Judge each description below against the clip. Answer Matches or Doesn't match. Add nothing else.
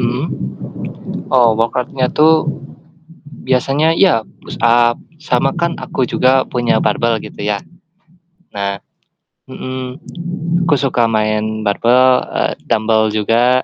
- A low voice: Matches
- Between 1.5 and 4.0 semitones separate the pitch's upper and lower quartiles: Matches